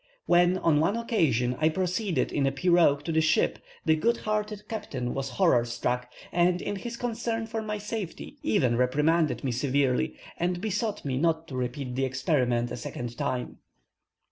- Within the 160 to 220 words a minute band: Yes, average, 170 wpm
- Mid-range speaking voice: Yes, medium, 160 Hz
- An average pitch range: No, wide, 7.5 semitones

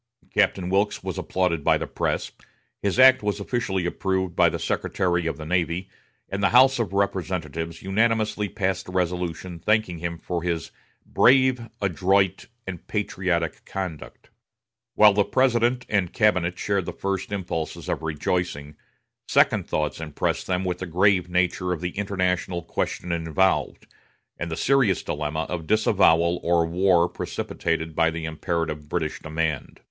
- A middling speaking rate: Yes, average, 150 wpm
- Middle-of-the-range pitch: No, very low, 90 Hz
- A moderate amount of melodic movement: Yes, average, 3.1 semitones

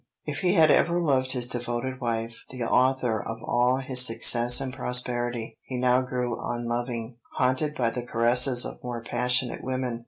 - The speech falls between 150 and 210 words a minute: Yes, average, 165 wpm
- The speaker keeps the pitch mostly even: Yes, narrow, 1.5 semitones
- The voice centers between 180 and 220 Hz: No, low, 125 Hz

